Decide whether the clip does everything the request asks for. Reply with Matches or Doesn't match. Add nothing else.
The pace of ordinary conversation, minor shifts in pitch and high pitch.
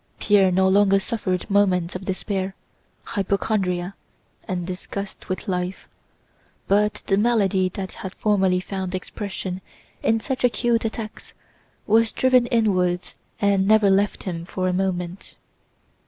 Doesn't match